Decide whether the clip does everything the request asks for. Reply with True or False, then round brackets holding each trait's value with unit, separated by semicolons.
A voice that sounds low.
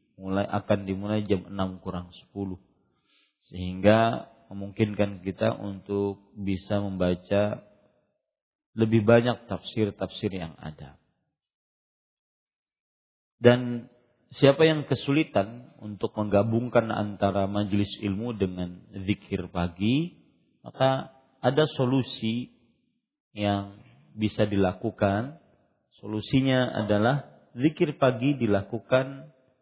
True (105 Hz)